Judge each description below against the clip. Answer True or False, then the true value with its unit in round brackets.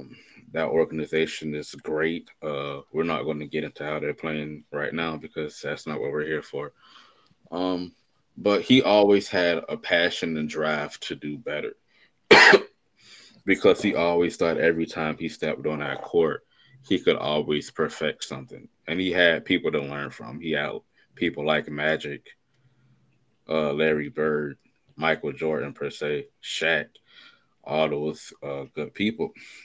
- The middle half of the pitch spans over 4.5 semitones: True (5.0 semitones)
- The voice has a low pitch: True (80 Hz)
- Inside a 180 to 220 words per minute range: False (155 wpm)